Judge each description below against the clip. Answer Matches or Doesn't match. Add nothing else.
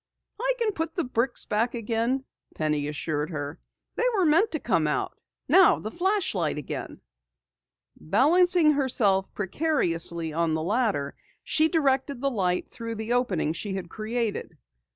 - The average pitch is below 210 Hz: Doesn't match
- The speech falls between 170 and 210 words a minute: Doesn't match